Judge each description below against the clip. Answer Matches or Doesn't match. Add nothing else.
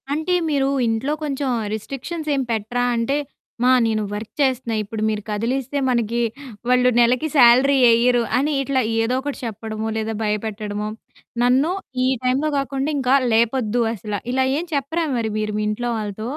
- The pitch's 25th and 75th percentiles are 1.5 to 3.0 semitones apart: Doesn't match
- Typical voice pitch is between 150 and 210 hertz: Doesn't match